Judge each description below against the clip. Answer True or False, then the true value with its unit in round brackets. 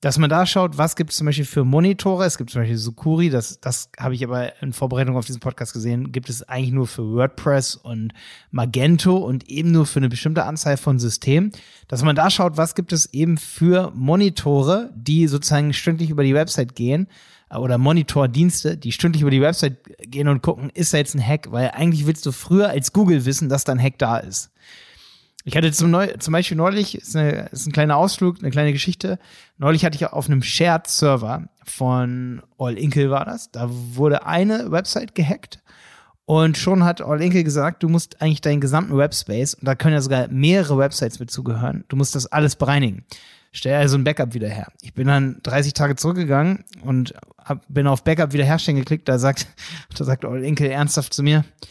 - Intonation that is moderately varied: True (4.0 semitones)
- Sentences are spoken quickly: True (200 wpm)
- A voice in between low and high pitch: True (145 Hz)